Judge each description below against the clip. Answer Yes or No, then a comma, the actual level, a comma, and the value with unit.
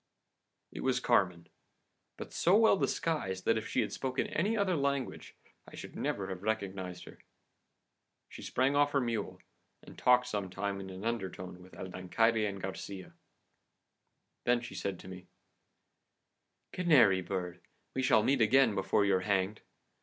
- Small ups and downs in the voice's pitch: No, wide, 5.5 semitones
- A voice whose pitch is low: Yes, low, 105 Hz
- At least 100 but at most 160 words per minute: Yes, average, 155 wpm